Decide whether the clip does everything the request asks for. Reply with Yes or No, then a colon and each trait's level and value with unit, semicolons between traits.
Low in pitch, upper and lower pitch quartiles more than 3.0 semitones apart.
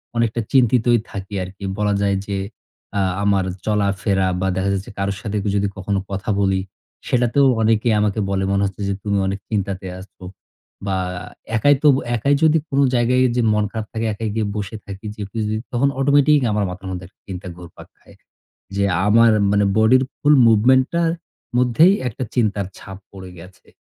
Yes: low, 105 Hz; average, 3.4 semitones